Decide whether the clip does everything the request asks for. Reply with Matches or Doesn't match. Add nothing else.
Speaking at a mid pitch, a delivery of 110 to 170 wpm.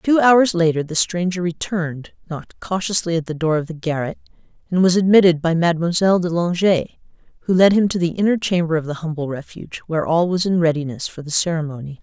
Doesn't match